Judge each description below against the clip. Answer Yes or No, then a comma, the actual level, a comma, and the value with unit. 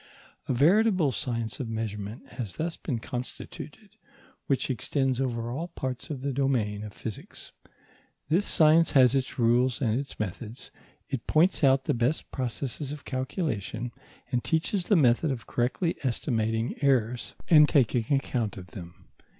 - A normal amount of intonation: Yes, average, 3.8 semitones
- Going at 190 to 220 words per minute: No, average, 150 wpm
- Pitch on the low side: Yes, low, 130 Hz